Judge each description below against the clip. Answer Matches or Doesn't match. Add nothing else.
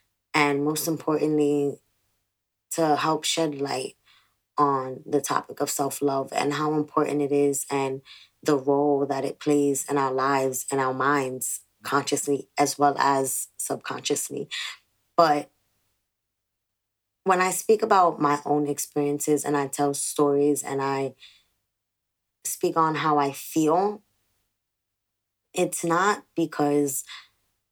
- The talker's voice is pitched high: Doesn't match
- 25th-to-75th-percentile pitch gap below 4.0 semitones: Doesn't match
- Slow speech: Matches